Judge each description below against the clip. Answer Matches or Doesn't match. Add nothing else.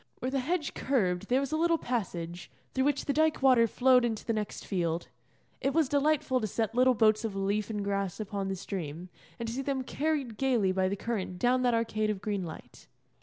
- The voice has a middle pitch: Doesn't match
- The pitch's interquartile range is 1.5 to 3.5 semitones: Doesn't match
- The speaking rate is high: Matches